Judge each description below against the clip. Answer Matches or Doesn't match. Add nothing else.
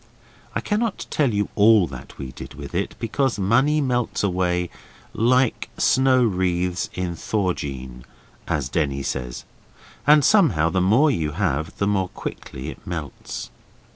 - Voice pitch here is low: Matches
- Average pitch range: Doesn't match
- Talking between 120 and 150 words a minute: Matches